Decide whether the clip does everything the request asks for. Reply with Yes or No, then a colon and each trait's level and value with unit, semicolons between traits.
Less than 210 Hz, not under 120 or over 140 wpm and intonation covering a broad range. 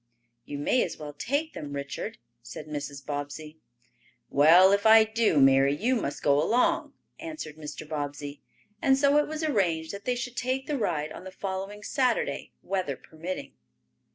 No: medium, 185 Hz; average, 165 wpm; wide, 9.0 semitones